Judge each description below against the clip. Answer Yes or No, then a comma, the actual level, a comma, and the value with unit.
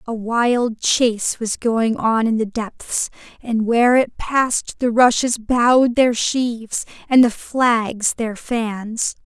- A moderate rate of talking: Yes, average, 150 wpm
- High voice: Yes, high, 230 Hz